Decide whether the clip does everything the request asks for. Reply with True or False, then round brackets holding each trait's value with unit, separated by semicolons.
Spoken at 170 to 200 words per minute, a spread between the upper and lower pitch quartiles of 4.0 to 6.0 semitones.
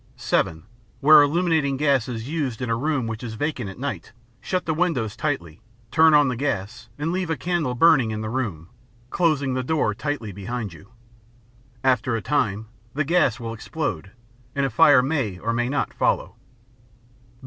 True (175 wpm; 5.0 semitones)